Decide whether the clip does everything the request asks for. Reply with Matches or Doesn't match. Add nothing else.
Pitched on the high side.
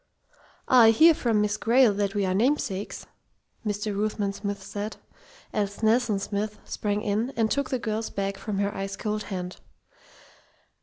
Matches